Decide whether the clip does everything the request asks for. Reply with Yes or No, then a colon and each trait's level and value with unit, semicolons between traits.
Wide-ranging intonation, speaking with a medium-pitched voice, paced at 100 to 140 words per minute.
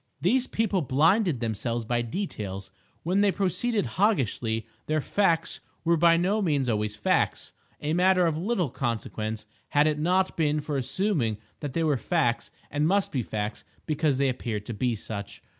No: wide, 7.6 semitones; medium, 150 Hz; average, 160 wpm